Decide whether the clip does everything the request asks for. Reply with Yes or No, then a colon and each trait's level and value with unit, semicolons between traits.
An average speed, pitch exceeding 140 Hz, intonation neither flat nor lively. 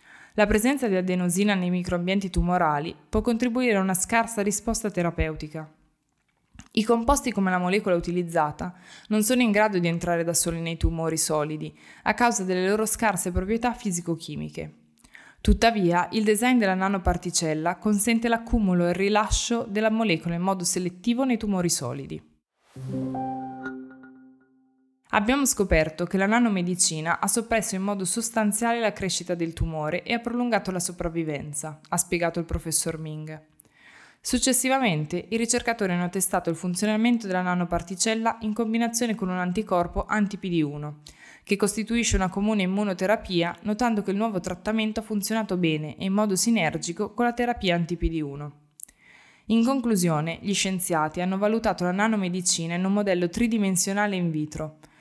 Yes: average, 140 wpm; medium, 185 Hz; average, 4.5 semitones